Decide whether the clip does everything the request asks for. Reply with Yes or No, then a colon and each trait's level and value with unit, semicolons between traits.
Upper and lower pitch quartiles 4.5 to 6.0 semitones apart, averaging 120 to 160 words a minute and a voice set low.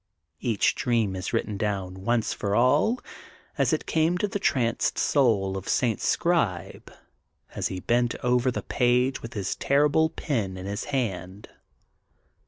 Yes: wide, 5.6 semitones; average, 150 wpm; low, 120 Hz